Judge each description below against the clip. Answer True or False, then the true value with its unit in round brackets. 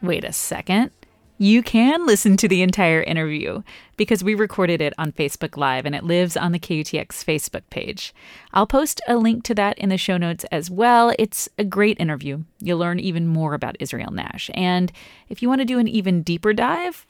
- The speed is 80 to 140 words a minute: False (205 wpm)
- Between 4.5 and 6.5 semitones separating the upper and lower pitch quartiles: True (5.0 semitones)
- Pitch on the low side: False (185 Hz)